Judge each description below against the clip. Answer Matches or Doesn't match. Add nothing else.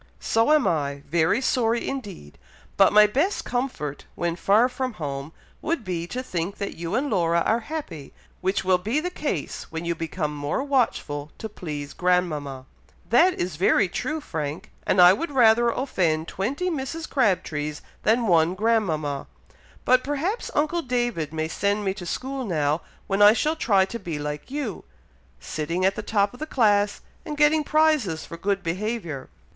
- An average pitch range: Doesn't match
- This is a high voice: Matches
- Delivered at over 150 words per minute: Matches